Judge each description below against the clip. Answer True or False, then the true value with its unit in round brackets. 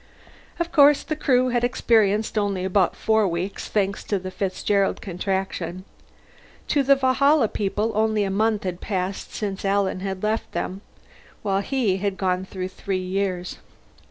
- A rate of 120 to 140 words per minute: False (155 wpm)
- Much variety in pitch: False (2.8 semitones)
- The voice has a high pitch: True (200 Hz)